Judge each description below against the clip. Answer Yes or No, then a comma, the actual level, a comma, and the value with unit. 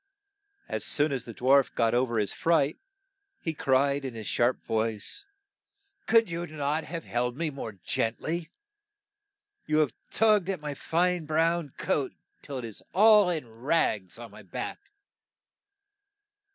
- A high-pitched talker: No, medium, 150 Hz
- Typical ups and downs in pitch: No, wide, 5.9 semitones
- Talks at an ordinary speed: Yes, average, 160 wpm